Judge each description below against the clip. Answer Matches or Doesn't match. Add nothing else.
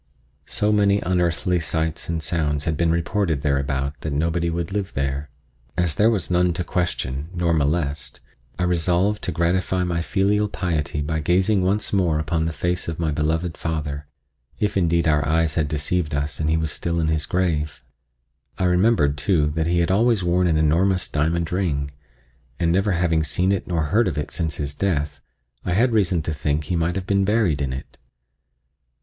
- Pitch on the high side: Doesn't match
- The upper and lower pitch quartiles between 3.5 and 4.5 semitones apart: Doesn't match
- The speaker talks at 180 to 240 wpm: Matches